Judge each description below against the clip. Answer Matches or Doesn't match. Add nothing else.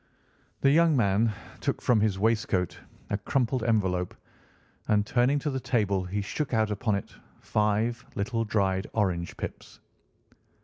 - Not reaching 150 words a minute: Matches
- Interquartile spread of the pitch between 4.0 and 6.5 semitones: Doesn't match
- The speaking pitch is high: Doesn't match